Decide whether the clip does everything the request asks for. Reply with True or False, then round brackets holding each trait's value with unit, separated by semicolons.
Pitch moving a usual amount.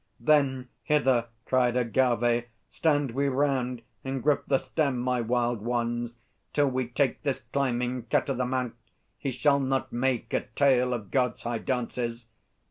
False (2.1 semitones)